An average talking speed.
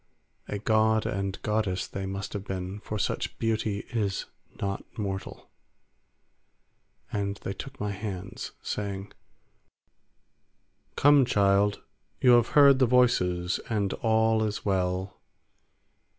No: slow, 115 wpm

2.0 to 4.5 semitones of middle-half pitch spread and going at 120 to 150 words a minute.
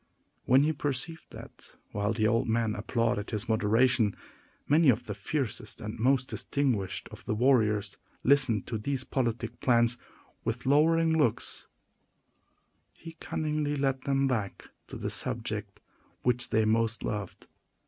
Yes: average, 4.0 semitones; average, 140 wpm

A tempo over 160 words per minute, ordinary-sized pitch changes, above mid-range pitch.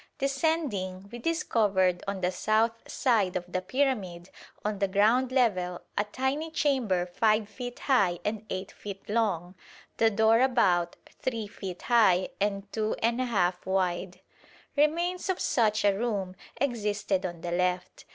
No: average, 140 wpm; average, 4.7 semitones; high, 210 Hz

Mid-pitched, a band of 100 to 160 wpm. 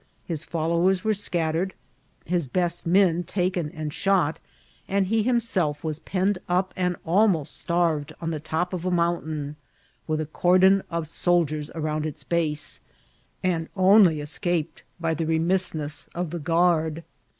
Yes: medium, 170 Hz; average, 150 wpm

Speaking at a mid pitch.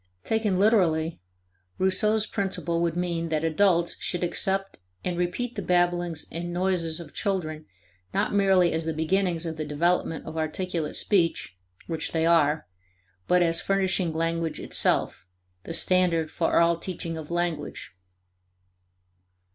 Yes: medium, 170 Hz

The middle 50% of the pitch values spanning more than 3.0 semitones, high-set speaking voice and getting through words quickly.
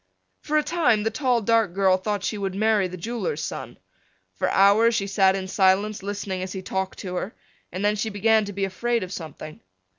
No: average, 2.7 semitones; high, 200 Hz; fast, 210 wpm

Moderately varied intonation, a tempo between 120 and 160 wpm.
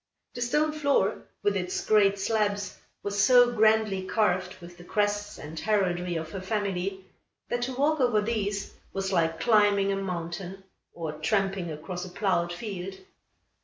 Yes: average, 3.2 semitones; average, 155 wpm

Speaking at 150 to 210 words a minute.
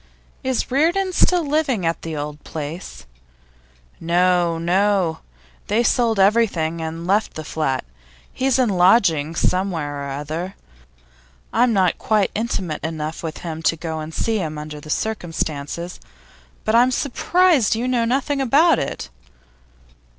No: average, 140 wpm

